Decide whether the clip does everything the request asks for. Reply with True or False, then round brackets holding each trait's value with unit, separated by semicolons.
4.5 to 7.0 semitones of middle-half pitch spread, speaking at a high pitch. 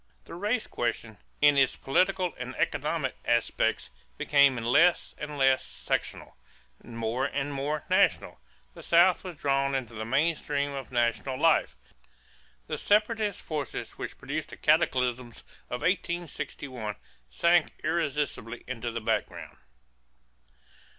False (5.1 semitones; 140 Hz)